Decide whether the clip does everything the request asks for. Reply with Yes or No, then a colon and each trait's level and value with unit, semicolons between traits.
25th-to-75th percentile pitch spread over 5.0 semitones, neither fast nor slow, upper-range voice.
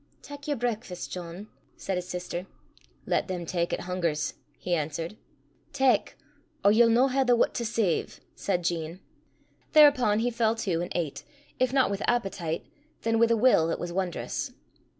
Yes: wide, 5.4 semitones; average, 170 wpm; high, 195 Hz